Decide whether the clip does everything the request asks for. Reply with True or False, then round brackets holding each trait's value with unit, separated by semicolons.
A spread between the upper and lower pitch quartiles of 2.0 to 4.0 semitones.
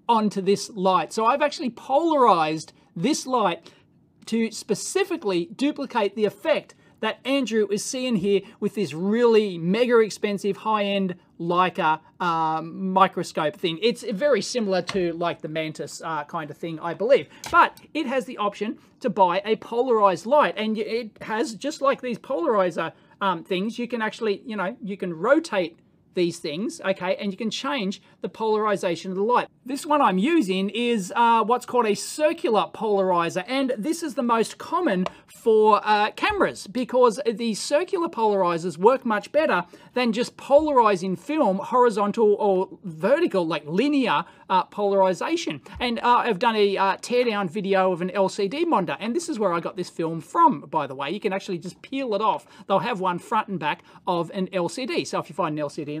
False (4.8 semitones)